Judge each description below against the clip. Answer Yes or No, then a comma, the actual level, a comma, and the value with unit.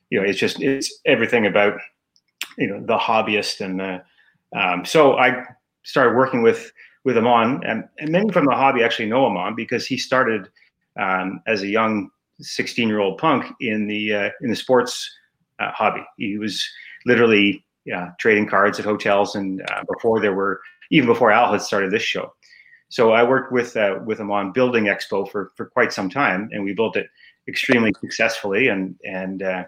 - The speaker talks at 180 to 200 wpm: Yes, average, 185 wpm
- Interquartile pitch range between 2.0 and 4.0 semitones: Yes, average, 3.5 semitones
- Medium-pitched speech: No, low, 105 Hz